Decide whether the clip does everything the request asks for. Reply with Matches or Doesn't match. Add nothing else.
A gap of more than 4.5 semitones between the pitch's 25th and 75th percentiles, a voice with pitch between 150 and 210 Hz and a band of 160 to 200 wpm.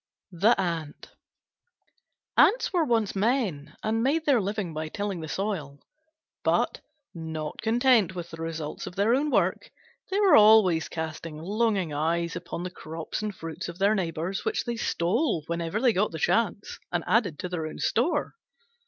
Matches